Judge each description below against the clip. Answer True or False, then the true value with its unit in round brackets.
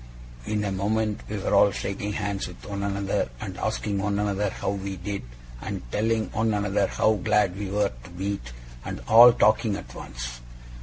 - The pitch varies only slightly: True (1.4 semitones)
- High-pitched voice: False (100 Hz)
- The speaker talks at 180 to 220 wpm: True (185 wpm)